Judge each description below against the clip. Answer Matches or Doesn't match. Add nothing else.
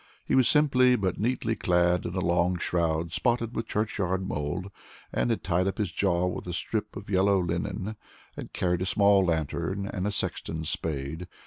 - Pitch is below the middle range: Matches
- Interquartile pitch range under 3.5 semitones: Matches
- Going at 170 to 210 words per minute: Matches